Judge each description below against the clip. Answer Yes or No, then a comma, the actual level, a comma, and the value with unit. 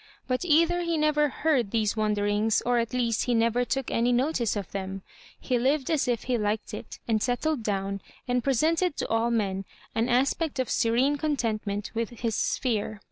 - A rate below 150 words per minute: No, average, 185 wpm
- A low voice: No, high, 240 Hz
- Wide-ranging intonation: No, average, 4.2 semitones